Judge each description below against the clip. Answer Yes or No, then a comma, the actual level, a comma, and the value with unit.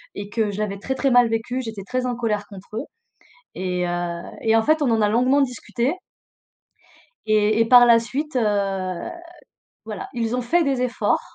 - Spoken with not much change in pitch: No, average, 3.5 semitones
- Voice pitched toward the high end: Yes, high, 230 Hz